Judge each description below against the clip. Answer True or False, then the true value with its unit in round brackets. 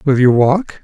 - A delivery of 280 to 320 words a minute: False (215 wpm)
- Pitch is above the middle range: False (140 Hz)